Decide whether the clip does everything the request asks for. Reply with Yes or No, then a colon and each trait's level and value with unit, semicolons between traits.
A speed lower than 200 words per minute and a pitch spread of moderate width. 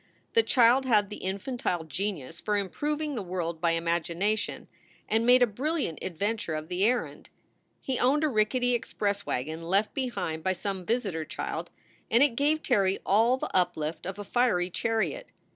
No: average, 165 wpm; wide, 5.8 semitones